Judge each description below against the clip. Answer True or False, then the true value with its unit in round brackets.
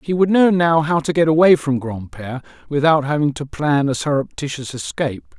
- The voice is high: False (145 Hz)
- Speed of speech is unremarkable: True (190 wpm)